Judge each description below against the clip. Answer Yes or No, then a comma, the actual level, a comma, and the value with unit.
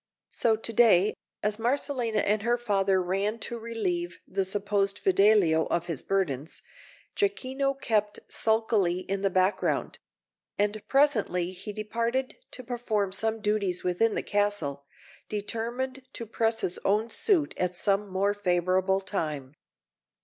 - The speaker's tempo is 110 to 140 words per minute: Yes, slow, 135 wpm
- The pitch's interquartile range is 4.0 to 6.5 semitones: No, average, 3.5 semitones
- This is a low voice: No, high, 205 Hz